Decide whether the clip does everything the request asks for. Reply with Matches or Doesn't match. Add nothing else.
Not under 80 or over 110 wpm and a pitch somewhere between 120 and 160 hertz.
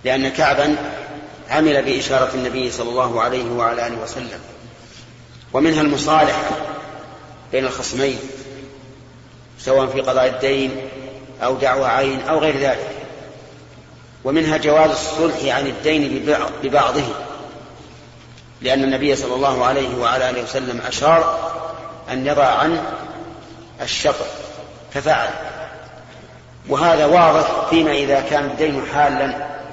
Matches